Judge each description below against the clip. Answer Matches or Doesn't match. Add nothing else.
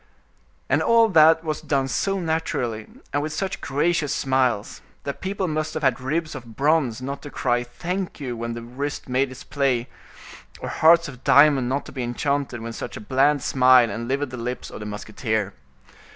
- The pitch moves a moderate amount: Matches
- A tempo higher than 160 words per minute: Matches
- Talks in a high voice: Doesn't match